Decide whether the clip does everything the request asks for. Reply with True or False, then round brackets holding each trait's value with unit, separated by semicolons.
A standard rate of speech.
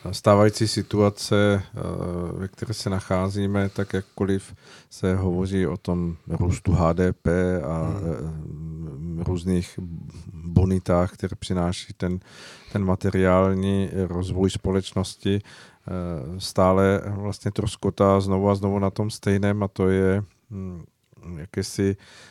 False (100 wpm)